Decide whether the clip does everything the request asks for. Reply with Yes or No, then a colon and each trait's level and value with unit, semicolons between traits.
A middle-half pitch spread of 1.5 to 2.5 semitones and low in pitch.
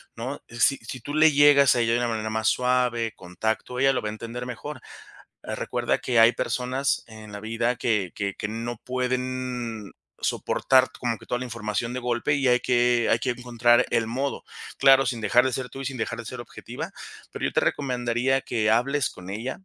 Yes: narrow, 2.0 semitones; low, 120 Hz